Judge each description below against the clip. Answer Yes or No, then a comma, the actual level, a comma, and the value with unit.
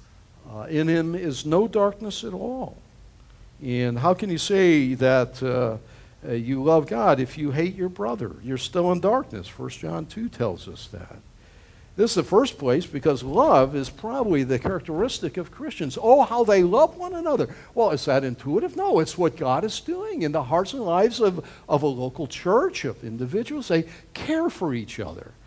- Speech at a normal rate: Yes, average, 190 wpm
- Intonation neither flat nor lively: No, wide, 8.1 semitones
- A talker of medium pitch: Yes, medium, 165 Hz